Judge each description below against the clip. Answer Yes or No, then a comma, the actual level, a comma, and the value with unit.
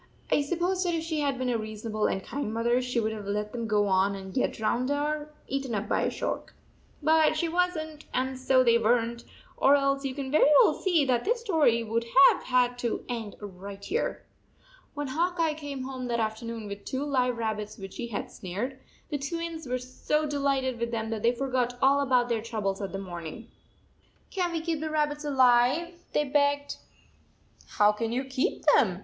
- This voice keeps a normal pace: No, fast, 220 wpm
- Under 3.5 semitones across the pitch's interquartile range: No, average, 4.6 semitones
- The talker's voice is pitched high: Yes, very high, 255 Hz